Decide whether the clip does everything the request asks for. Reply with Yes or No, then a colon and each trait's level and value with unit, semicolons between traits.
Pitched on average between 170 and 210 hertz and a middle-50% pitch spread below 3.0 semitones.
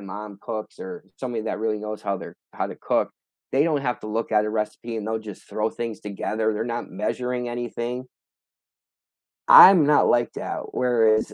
No: low, 110 Hz; narrow, 2.4 semitones